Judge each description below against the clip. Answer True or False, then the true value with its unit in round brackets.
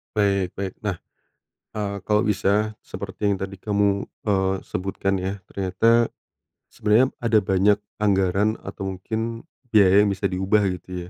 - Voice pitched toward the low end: True (100 Hz)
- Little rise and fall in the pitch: True (1.8 semitones)